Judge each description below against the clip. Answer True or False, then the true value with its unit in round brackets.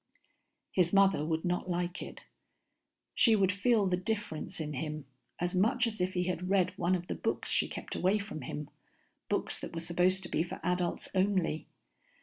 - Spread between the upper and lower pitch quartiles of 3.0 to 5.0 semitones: False (2.4 semitones)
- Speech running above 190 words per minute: False (185 wpm)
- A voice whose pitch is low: False (180 Hz)